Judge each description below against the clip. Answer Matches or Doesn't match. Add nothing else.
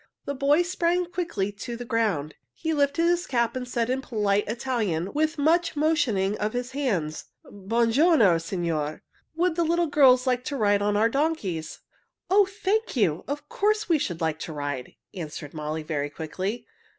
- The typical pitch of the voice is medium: Doesn't match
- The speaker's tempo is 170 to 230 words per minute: Matches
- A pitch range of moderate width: Doesn't match